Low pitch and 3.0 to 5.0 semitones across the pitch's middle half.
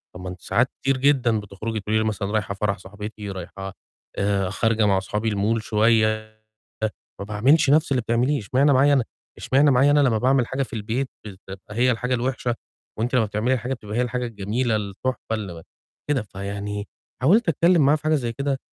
Yes: low, 115 Hz; average, 4.2 semitones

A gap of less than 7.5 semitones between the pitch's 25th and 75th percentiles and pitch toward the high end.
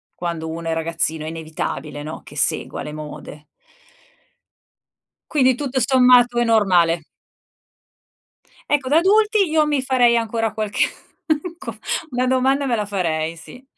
No: wide, 8.0 semitones; high, 230 Hz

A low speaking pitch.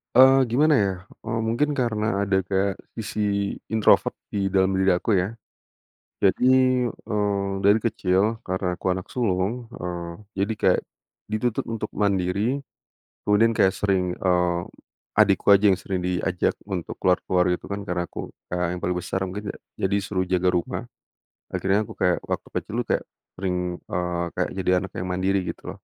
Yes: very low, 95 Hz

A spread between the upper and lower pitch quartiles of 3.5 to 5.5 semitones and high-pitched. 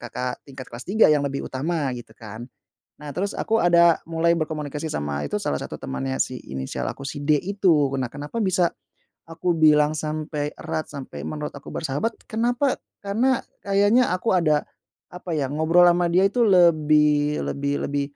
No: average, 4.1 semitones; medium, 155 Hz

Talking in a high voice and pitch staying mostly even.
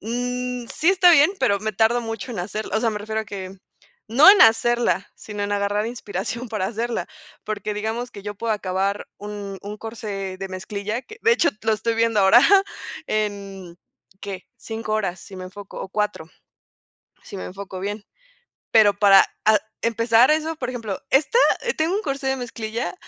No: high, 215 Hz; average, 3.0 semitones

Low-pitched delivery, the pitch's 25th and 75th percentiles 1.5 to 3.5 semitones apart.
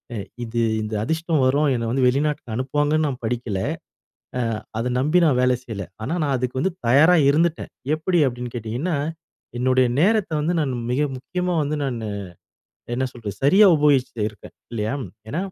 No: low, 130 Hz; average, 4.3 semitones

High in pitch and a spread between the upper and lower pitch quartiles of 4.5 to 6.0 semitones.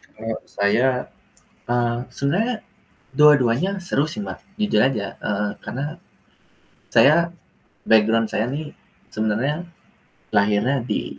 No: low, 125 Hz; wide, 5.5 semitones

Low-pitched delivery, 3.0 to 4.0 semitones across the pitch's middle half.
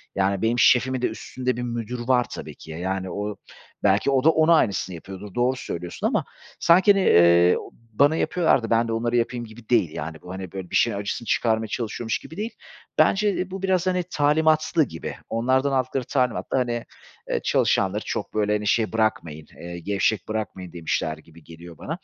No: low, 115 Hz; wide, 5.4 semitones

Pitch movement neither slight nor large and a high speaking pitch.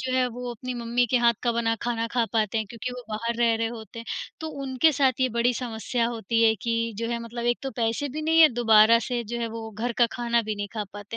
No: narrow, 1.5 semitones; high, 235 Hz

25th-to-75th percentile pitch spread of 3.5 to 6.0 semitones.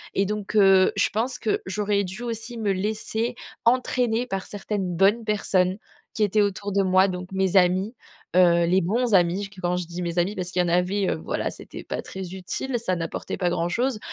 No: average, 2.9 semitones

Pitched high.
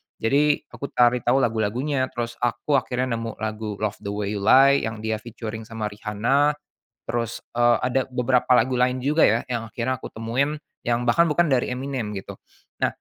No: low, 120 Hz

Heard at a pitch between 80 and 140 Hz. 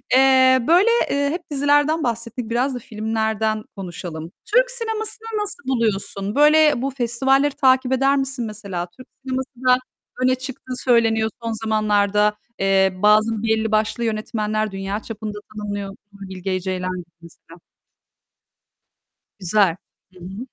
No: high, 220 Hz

